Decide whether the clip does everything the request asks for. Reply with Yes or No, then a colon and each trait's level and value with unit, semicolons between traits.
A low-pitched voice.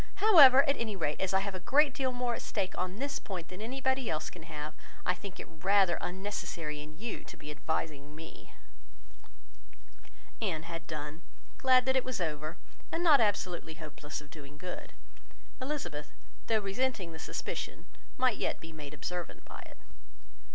No: medium, 185 Hz